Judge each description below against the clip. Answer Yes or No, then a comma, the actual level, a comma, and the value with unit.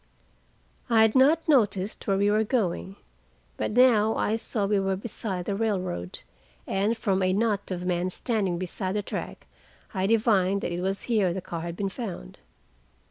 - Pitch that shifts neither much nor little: Yes, average, 3.0 semitones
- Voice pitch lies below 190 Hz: No, high, 200 Hz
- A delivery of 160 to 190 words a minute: Yes, average, 175 wpm